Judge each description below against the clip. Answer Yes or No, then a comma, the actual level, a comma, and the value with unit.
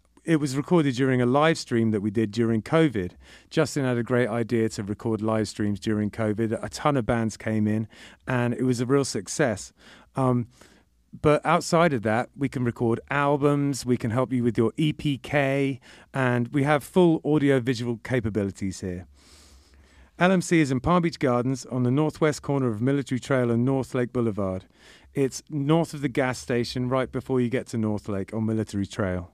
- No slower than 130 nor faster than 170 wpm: No, average, 190 wpm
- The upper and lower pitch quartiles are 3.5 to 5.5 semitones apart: Yes, average, 4.2 semitones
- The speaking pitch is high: No, low, 125 Hz